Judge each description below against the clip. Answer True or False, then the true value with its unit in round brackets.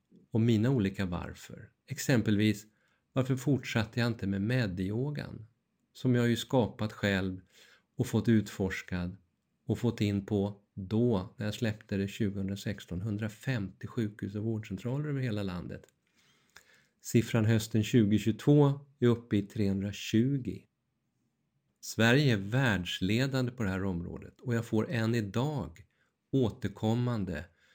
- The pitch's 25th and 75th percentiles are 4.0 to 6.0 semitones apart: False (3.4 semitones)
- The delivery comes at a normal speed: False (120 wpm)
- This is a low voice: True (110 Hz)